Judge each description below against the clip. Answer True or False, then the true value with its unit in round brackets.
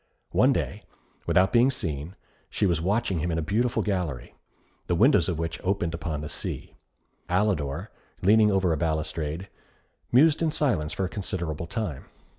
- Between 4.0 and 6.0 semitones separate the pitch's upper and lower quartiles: True (4.7 semitones)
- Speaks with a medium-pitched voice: False (90 Hz)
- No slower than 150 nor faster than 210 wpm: True (160 wpm)